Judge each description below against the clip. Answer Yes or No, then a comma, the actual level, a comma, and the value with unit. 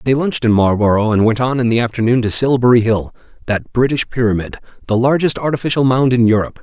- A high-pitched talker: No, low, 120 Hz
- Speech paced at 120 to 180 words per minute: No, average, 200 wpm